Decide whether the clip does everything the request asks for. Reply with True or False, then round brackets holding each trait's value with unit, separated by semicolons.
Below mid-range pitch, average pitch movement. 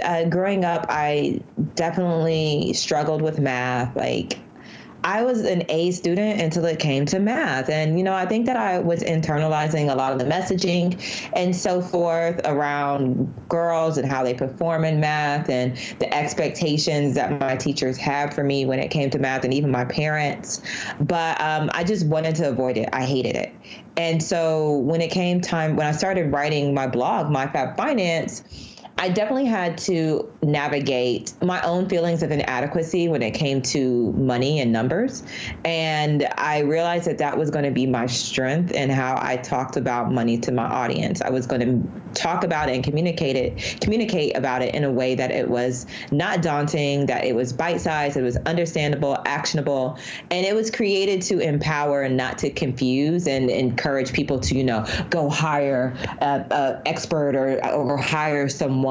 False (150 Hz; 4.2 semitones)